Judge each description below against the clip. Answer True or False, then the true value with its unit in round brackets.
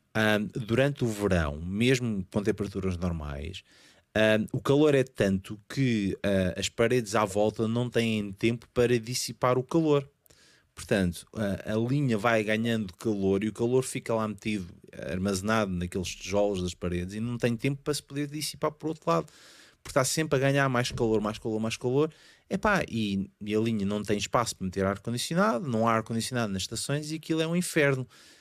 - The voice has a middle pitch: False (115 Hz)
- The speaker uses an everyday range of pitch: True (4.5 semitones)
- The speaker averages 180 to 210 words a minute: True (185 wpm)